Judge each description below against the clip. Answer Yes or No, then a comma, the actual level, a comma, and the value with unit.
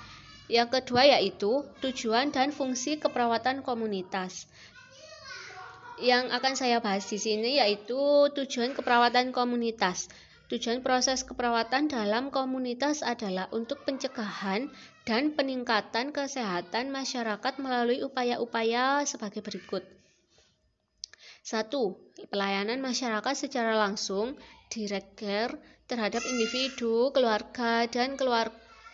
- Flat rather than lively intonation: No, average, 3.3 semitones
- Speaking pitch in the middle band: No, high, 240 Hz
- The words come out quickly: No, average, 95 wpm